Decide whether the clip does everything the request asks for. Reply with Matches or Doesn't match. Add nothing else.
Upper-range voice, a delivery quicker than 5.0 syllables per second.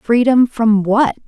Doesn't match